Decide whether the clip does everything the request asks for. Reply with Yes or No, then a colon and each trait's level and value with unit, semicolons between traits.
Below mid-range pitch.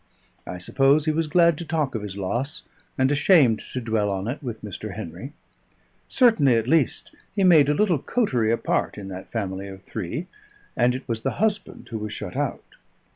Yes: low, 125 Hz